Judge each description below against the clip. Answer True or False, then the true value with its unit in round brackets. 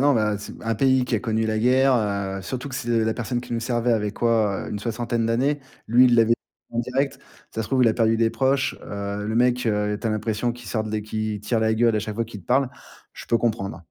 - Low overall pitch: True (115 Hz)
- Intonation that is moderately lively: False (2.2 semitones)